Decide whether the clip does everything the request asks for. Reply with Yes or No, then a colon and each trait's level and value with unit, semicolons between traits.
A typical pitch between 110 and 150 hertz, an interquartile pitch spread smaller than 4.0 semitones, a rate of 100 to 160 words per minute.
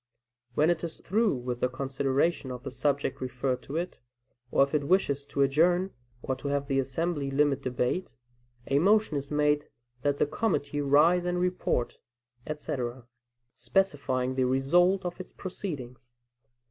No: medium, 140 Hz; average, 4.8 semitones; average, 155 wpm